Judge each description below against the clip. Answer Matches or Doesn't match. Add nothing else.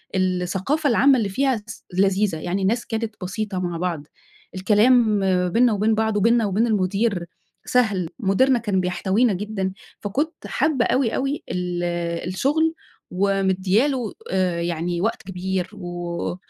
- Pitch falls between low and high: Doesn't match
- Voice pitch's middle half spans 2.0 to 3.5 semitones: Doesn't match